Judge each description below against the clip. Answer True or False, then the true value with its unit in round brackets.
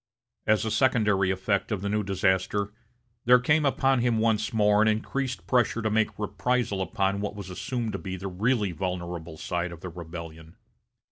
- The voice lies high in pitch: False (105 Hz)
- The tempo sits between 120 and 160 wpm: False (180 wpm)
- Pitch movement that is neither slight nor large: True (3.3 semitones)